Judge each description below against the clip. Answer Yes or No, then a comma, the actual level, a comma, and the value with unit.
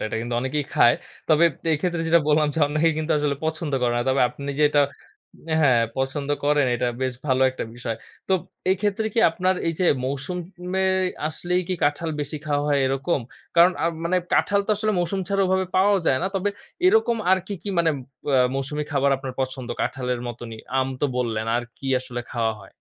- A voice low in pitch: No, medium, 145 Hz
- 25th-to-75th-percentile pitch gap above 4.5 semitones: Yes, average, 5.2 semitones